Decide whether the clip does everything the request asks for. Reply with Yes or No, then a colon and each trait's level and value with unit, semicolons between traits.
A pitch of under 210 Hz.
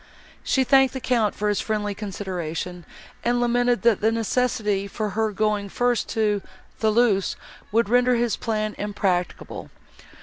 No: high, 215 Hz